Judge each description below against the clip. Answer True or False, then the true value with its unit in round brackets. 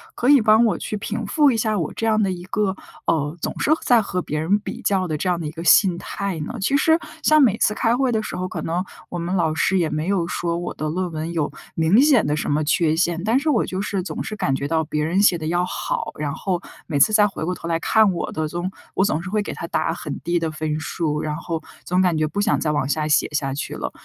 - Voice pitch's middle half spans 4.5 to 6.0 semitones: True (4.8 semitones)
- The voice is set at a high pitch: False (175 Hz)